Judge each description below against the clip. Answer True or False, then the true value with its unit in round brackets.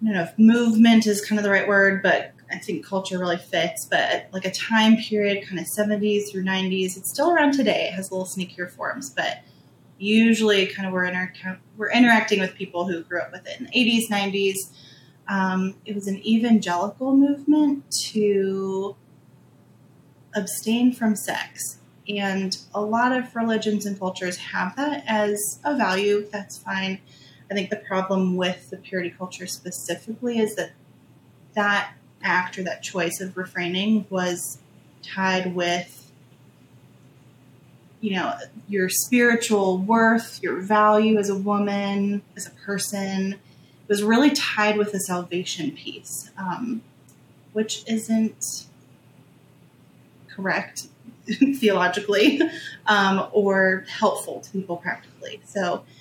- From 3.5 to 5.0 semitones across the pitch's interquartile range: False (3.0 semitones)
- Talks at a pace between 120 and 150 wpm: True (145 wpm)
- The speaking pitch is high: True (195 Hz)